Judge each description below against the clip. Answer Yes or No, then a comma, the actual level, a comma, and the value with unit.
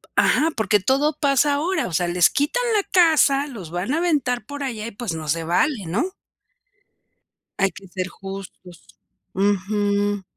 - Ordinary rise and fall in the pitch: No, wide, 7.4 semitones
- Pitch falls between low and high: No, high, 215 Hz